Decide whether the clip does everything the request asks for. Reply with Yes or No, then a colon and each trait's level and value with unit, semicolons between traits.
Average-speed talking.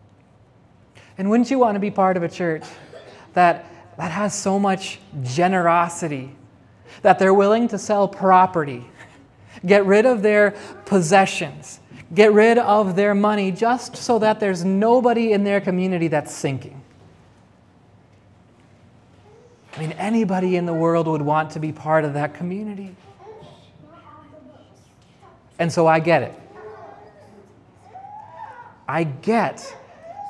No: slow, 125 wpm